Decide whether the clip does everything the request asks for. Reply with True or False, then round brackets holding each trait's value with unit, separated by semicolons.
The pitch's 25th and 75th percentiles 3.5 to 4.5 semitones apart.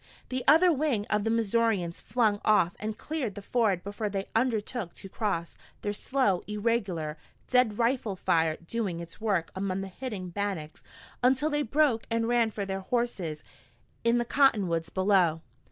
True (4.1 semitones)